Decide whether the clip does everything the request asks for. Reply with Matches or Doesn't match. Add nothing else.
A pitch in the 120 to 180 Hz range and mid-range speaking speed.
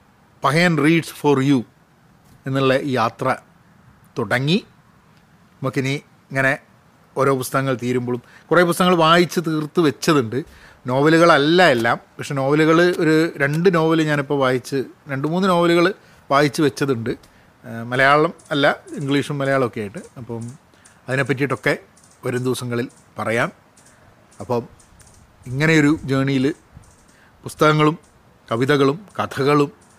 Matches